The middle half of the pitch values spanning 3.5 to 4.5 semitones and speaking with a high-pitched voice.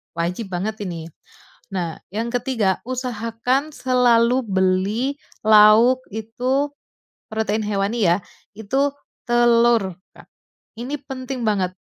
Yes: average, 3.9 semitones; high, 225 Hz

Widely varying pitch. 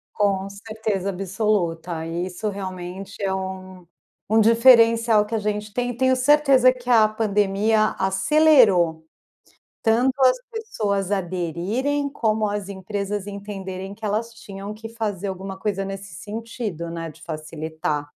No: average, 3.1 semitones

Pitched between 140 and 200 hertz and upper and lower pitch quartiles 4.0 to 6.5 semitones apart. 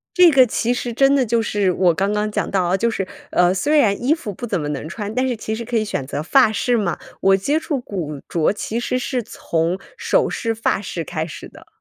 No: high, 215 Hz; average, 5.1 semitones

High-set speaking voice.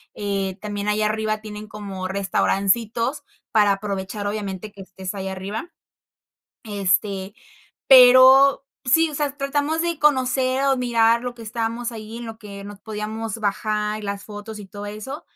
Yes: high, 215 Hz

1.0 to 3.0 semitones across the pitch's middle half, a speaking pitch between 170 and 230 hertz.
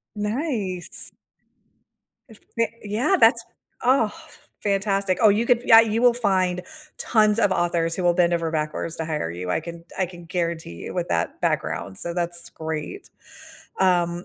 No: average, 4.3 semitones; medium, 185 Hz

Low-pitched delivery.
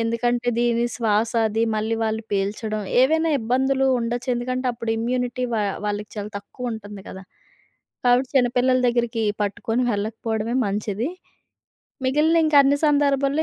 No: high, 235 Hz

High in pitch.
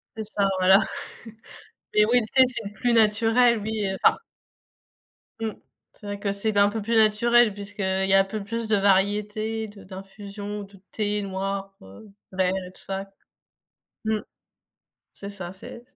Yes: high, 205 Hz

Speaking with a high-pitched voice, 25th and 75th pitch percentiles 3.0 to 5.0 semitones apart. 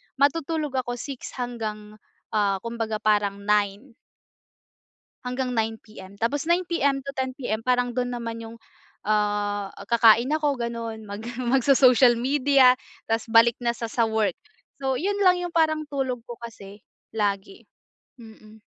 Yes: high, 235 Hz; average, 3.6 semitones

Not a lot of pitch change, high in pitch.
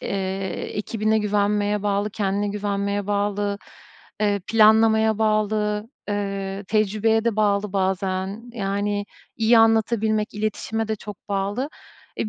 Yes: narrow, 1.4 semitones; high, 205 Hz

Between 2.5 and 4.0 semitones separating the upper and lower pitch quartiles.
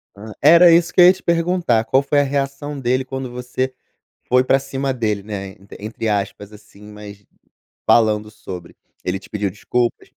No: average, 4.8 semitones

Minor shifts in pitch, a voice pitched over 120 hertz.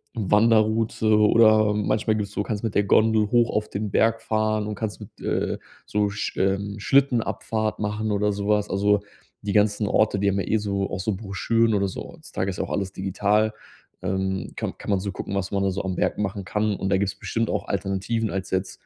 No: narrow, 1.7 semitones; low, 105 Hz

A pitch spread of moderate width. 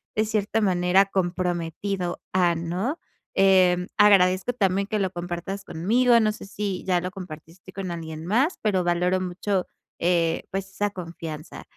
No: narrow, 2.3 semitones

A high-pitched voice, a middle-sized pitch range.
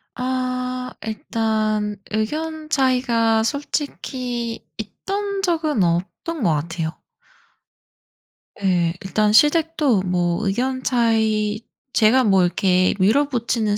Yes: high, 225 Hz; average, 4.2 semitones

